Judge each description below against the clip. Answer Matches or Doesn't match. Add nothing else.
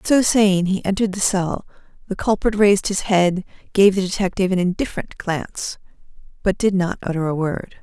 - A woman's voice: Matches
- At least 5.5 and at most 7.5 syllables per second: Matches